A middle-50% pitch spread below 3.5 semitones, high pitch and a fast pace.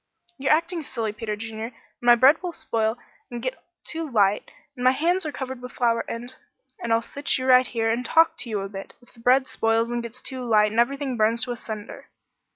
Yes: average, 2.7 semitones; high, 240 Hz; fast, 245 wpm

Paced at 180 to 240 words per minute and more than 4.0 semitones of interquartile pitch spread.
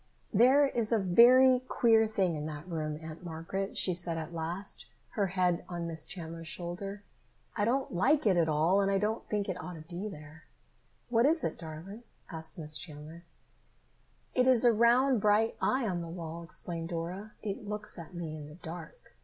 Yes: average, 190 wpm; average, 4.8 semitones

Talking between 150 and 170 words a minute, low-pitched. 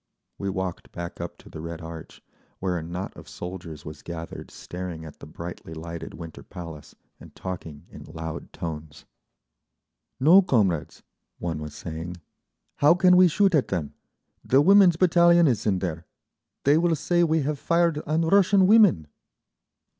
Yes: average, 155 wpm; very low, 95 Hz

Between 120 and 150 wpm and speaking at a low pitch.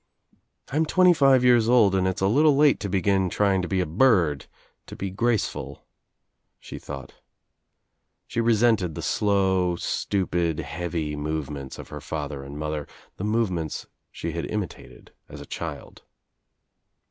Yes: average, 145 wpm; very low, 95 Hz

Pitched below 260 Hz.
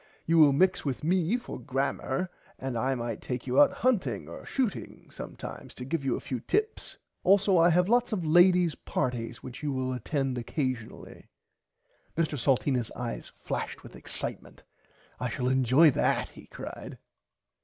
Yes: medium, 140 Hz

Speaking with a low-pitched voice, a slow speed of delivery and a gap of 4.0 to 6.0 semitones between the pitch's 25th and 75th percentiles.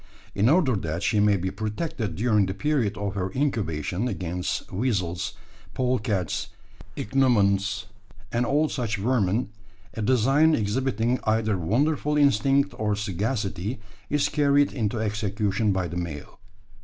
Yes: low, 110 Hz; slow, 130 wpm; average, 4.8 semitones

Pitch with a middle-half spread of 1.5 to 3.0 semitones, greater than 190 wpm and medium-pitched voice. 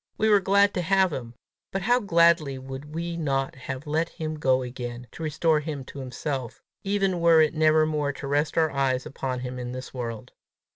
No: average, 4.3 semitones; average, 200 wpm; medium, 150 Hz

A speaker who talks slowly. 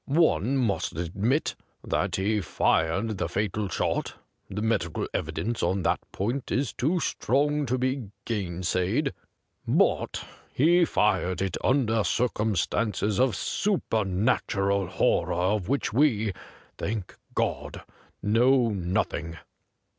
Yes: slow, 115 wpm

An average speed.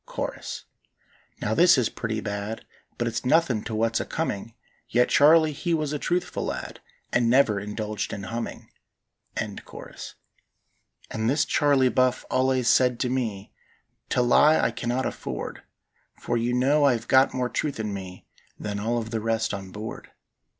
Yes: average, 160 wpm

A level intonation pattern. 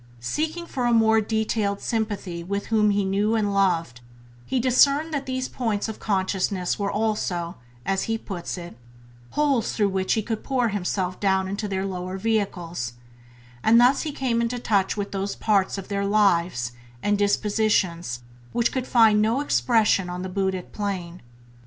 No: average, 3.1 semitones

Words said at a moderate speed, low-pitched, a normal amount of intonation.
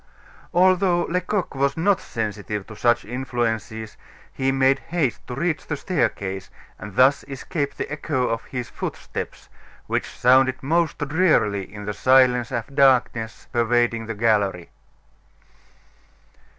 No: slow, 125 wpm; low, 130 Hz; average, 4.5 semitones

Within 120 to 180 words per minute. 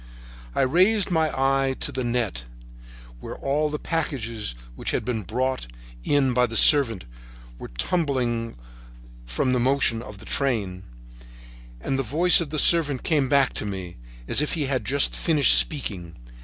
Yes: average, 160 wpm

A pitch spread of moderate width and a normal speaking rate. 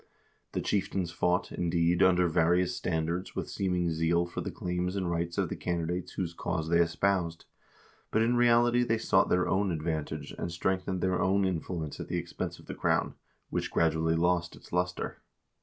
No: narrow, 1.9 semitones; average, 175 wpm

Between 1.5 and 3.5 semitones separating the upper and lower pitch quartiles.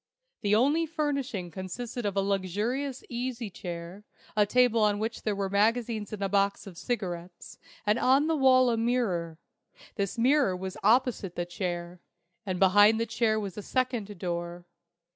No: average, 4.6 semitones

